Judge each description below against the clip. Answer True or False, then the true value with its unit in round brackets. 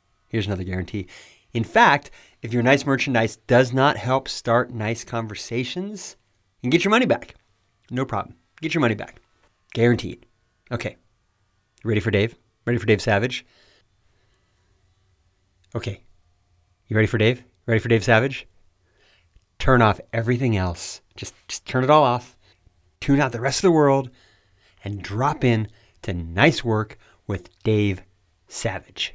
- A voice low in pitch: True (110 Hz)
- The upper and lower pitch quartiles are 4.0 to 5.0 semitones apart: True (4.3 semitones)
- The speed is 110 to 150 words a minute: True (145 wpm)